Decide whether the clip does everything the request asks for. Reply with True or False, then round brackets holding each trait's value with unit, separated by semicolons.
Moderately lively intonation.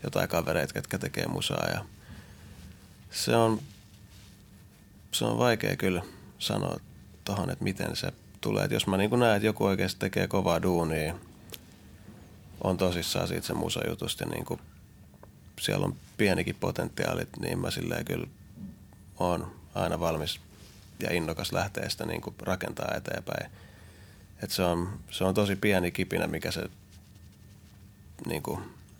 False (1.9 semitones)